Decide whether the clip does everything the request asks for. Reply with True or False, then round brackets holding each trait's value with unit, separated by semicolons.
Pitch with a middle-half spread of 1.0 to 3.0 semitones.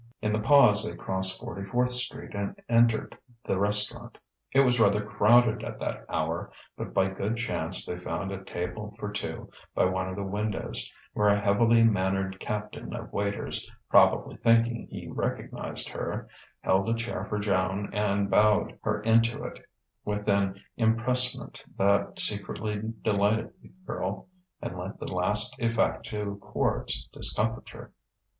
True (2.5 semitones)